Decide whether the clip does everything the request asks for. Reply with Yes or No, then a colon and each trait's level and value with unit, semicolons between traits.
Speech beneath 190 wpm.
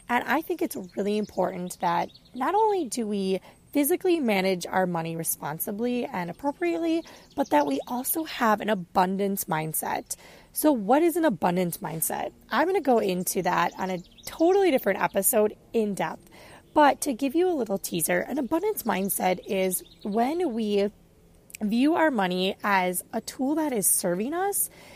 Yes: average, 160 wpm